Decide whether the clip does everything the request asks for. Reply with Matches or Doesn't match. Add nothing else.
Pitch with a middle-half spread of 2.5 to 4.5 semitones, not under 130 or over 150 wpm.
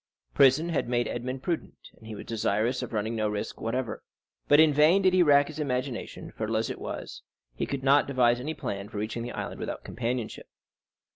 Doesn't match